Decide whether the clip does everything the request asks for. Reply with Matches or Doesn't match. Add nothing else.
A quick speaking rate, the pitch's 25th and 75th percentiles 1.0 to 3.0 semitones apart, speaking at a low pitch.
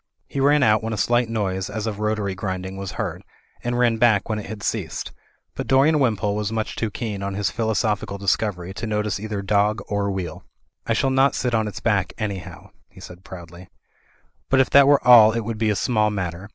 Matches